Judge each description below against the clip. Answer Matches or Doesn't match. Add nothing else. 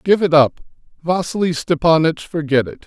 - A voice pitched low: Doesn't match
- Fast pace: Doesn't match